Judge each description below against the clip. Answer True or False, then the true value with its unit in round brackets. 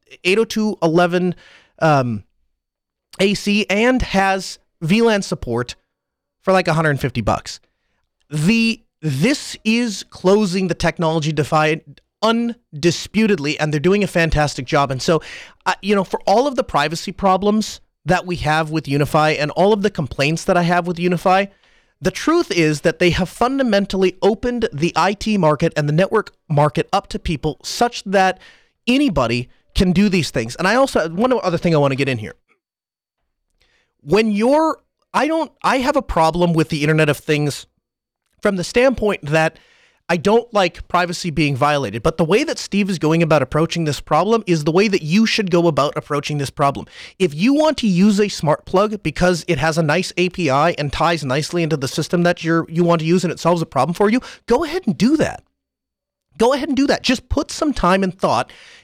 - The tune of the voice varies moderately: True (5.0 semitones)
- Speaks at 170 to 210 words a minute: True (185 wpm)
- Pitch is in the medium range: True (175 Hz)